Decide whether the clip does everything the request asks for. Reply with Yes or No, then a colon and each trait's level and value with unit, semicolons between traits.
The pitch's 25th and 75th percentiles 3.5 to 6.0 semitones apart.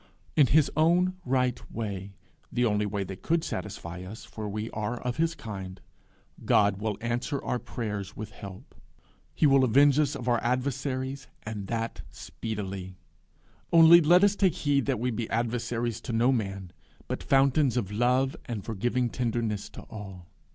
Yes: average, 4.4 semitones